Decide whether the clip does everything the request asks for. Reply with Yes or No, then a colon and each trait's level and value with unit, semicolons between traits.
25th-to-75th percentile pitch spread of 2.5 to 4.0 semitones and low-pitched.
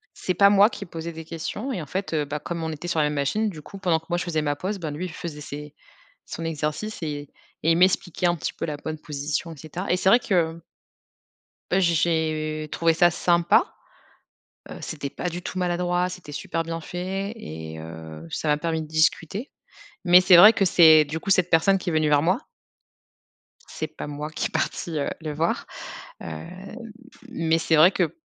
No: average, 2.8 semitones; medium, 165 Hz